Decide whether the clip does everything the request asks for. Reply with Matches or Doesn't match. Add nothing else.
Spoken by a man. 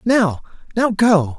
Matches